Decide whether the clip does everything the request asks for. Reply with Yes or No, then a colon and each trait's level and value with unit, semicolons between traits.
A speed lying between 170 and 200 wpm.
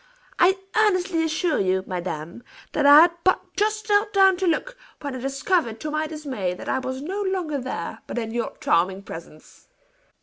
Yes: average, 180 wpm